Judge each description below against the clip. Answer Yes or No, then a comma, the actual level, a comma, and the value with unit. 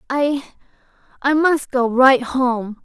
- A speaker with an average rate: No, slow, 85 wpm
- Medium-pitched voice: No, very high, 265 Hz